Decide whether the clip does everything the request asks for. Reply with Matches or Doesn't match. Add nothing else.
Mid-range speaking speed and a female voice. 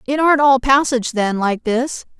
Matches